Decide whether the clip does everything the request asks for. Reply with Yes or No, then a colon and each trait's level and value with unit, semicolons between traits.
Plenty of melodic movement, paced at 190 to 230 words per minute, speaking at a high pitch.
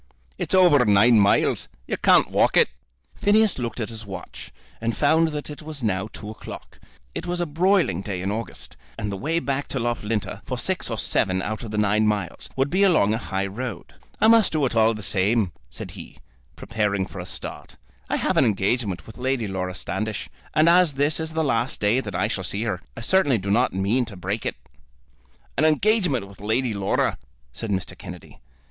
No: wide, 6.6 semitones; fast, 205 wpm; low, 115 Hz